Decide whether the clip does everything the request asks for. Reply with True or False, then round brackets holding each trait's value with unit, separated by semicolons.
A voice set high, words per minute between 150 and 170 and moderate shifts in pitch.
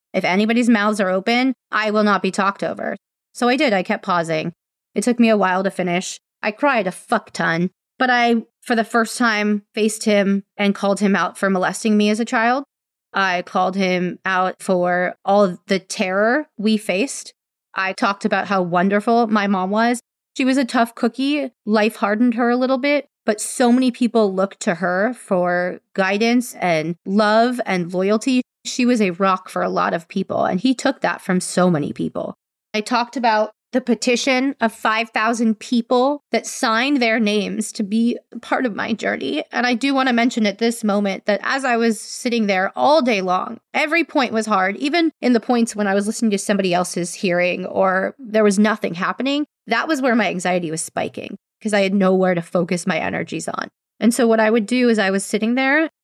False (215 Hz; 205 wpm; 3.9 semitones)